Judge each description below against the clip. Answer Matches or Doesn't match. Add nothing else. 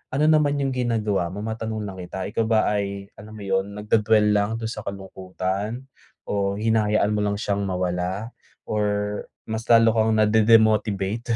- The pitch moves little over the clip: Matches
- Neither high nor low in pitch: Doesn't match